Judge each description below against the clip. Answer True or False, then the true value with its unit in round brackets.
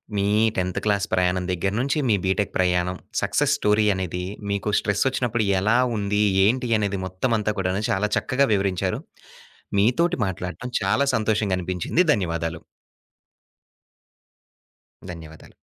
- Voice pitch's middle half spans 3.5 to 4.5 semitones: False (2.9 semitones)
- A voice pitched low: True (100 Hz)